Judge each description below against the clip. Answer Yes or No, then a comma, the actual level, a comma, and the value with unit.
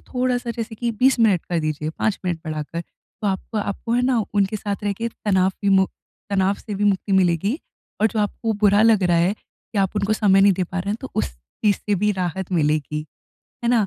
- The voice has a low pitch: No, high, 200 Hz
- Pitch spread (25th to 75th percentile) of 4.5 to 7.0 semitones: No, average, 3.2 semitones